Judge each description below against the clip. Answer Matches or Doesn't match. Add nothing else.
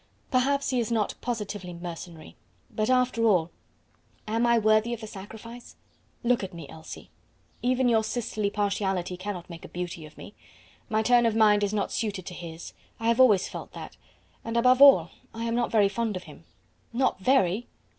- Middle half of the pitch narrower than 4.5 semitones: Matches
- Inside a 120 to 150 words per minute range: Doesn't match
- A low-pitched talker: Doesn't match